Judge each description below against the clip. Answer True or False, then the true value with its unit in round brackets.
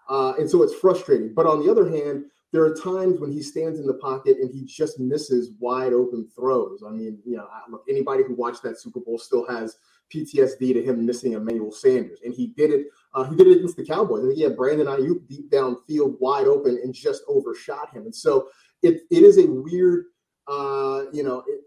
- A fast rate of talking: True (225 wpm)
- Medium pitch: True (150 Hz)